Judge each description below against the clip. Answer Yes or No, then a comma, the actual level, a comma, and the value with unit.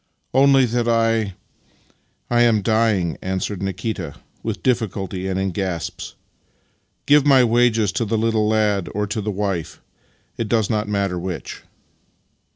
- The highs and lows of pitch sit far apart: No, average, 3.1 semitones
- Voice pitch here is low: Yes, low, 105 Hz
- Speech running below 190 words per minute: Yes, average, 160 wpm